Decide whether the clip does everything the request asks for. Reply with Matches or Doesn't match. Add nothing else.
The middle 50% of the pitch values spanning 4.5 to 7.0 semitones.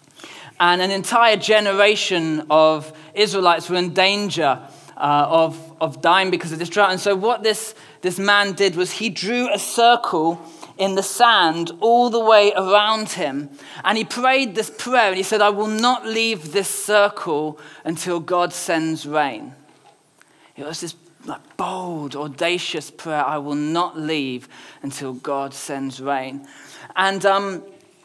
Matches